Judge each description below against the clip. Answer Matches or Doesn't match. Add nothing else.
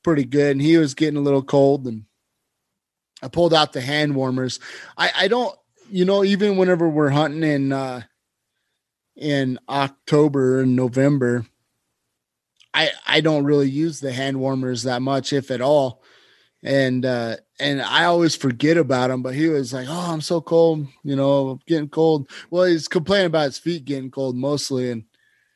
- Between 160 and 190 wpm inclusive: Matches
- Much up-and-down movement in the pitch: Doesn't match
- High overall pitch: Doesn't match